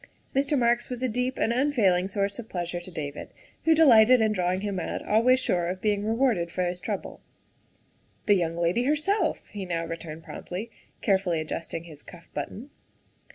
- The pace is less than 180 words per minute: No, average, 185 wpm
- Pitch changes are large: Yes, wide, 6.0 semitones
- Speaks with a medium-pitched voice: No, high, 200 Hz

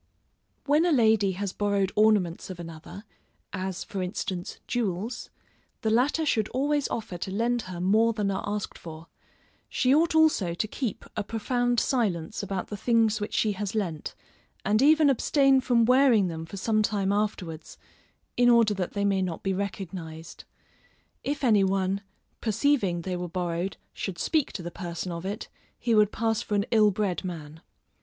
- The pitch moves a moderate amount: Yes, average, 4.0 semitones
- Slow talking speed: No, average, 170 wpm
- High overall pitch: Yes, high, 205 Hz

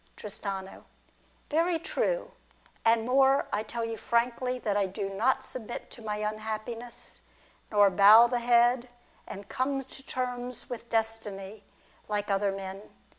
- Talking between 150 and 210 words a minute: No, slow, 135 wpm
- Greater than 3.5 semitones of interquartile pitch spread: No, average, 3.2 semitones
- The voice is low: No, high, 225 Hz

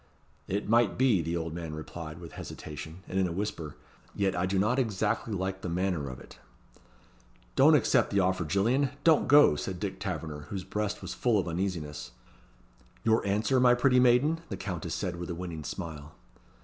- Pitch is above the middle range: No, very low, 95 Hz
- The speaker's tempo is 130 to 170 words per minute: No, average, 185 wpm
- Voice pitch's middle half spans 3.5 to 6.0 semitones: Yes, average, 4.4 semitones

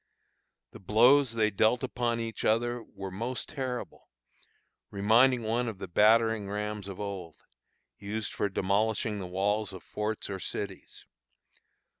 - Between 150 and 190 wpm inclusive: No, slow, 135 wpm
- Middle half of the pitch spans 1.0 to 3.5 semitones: Yes, average, 2.7 semitones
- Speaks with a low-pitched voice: Yes, low, 110 Hz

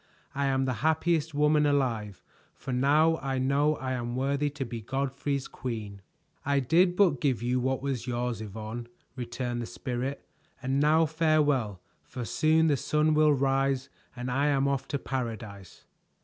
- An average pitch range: Yes, average, 3.2 semitones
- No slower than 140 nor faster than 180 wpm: Yes, average, 165 wpm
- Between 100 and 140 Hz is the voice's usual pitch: Yes, low, 135 Hz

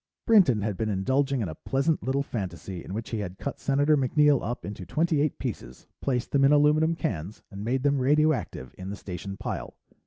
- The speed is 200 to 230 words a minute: Yes, fast, 205 wpm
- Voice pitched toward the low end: Yes, low, 130 Hz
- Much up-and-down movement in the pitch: Yes, wide, 6.2 semitones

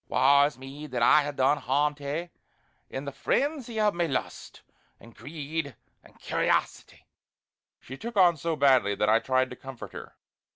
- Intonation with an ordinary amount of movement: Yes, average, 3.7 semitones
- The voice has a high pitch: No, medium, 145 Hz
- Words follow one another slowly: No, average, 175 wpm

